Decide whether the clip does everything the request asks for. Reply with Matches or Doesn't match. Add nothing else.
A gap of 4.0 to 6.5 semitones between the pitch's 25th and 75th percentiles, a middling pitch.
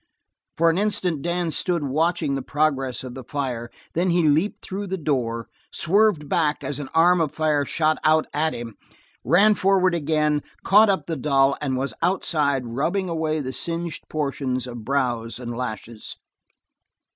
Matches